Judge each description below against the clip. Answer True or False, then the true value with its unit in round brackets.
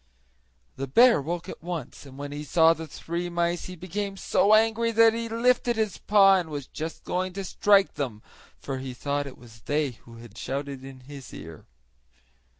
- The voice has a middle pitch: True (160 Hz)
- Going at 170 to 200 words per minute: True (190 wpm)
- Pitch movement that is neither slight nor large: False (6.4 semitones)